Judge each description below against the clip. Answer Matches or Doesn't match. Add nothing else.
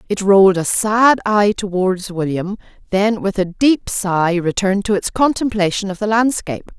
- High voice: Matches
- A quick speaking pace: Doesn't match